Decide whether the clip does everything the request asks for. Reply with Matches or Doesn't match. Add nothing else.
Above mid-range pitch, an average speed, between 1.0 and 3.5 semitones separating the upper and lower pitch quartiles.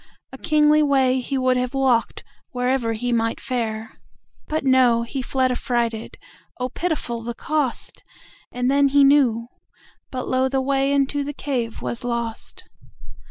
Doesn't match